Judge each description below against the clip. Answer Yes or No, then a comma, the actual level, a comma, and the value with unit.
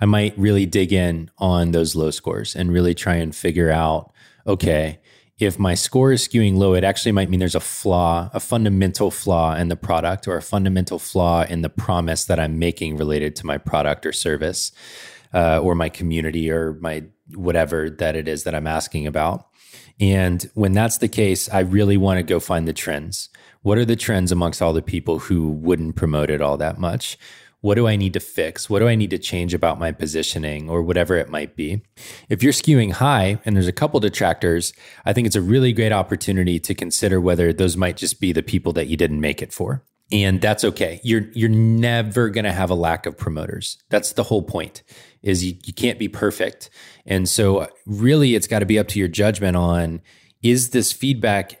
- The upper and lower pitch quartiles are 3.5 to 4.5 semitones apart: Yes, average, 4.1 semitones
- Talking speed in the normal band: No, fast, 210 wpm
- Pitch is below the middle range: Yes, very low, 95 Hz